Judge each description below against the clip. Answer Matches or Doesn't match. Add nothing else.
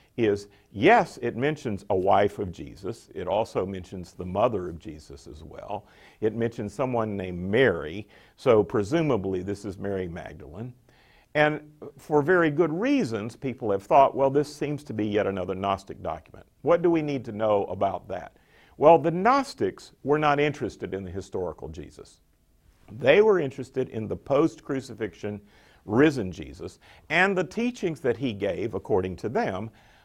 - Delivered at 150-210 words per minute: Matches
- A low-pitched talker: Matches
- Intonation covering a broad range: Matches